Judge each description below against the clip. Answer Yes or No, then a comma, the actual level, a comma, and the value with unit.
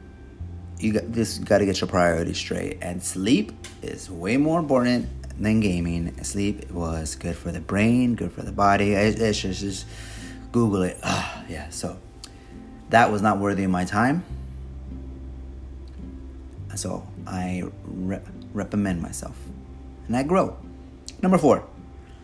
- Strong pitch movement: Yes, wide, 7.1 semitones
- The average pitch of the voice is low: Yes, very low, 90 Hz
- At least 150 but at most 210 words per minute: No, slow, 135 wpm